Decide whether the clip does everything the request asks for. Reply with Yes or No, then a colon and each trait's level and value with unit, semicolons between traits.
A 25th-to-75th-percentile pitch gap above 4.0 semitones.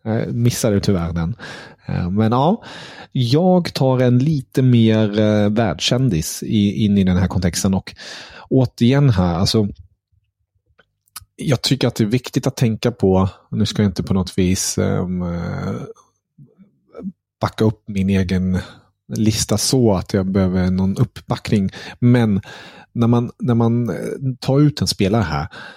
Yes: average, 4.5 semitones